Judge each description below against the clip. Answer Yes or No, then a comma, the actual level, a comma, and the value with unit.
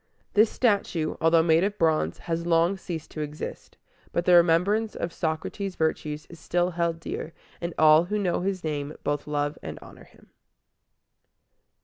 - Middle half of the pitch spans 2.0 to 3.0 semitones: Yes, narrow, 2.4 semitones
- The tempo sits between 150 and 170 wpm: Yes, average, 160 wpm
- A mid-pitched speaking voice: Yes, medium, 165 Hz